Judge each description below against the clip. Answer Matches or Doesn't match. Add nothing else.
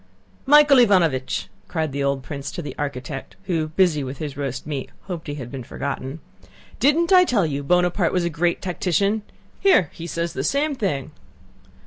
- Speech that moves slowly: Doesn't match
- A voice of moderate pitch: Matches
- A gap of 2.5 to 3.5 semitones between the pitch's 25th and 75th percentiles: Doesn't match